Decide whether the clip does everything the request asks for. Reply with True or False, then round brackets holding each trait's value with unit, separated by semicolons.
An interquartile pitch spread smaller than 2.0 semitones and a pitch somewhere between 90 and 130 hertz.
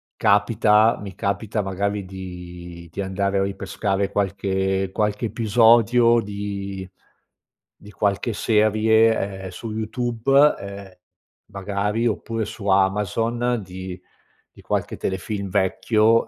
False (2.5 semitones; 100 Hz)